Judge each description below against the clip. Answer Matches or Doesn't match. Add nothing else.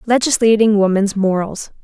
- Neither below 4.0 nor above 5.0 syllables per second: Matches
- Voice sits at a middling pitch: Doesn't match